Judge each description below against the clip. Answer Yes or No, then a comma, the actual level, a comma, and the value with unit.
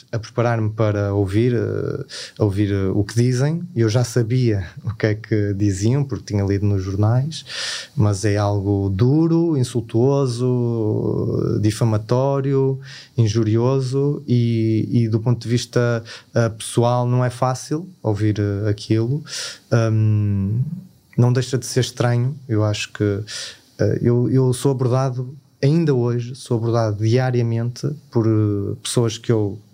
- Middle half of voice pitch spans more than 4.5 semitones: No, average, 3.2 semitones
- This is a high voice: No, low, 120 Hz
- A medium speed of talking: Yes, average, 135 wpm